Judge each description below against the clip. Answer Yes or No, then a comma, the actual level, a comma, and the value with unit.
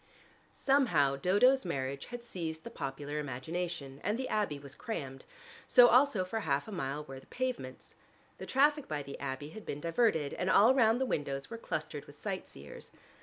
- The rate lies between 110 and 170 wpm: No, average, 180 wpm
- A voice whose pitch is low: No, medium, 165 Hz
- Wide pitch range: Yes, wide, 8.5 semitones